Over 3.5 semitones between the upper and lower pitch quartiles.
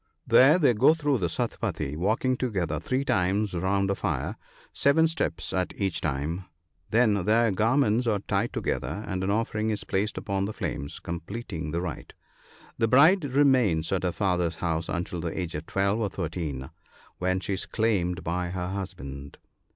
Yes: average, 4.7 semitones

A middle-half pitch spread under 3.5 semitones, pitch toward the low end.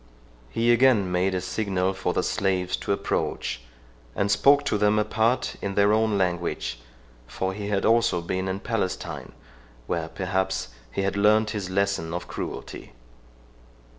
Yes: narrow, 2.6 semitones; low, 100 Hz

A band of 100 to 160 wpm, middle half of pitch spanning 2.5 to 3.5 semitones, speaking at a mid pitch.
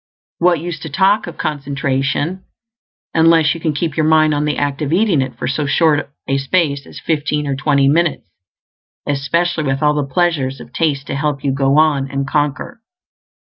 No: average, 180 wpm; average, 2.9 semitones; medium, 150 Hz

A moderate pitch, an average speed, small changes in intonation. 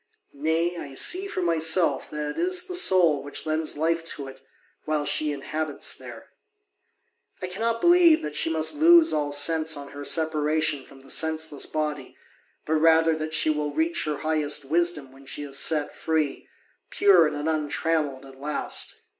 Yes: medium, 155 Hz; average, 170 wpm; narrow, 2.3 semitones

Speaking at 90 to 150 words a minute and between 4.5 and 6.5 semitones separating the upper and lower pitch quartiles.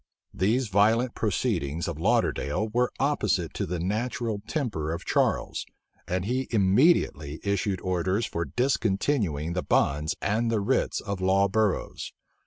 Yes: slow, 135 wpm; average, 4.9 semitones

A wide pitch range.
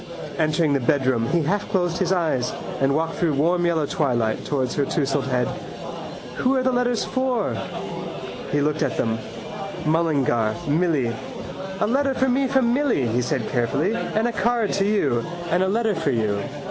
Yes: wide, 8.1 semitones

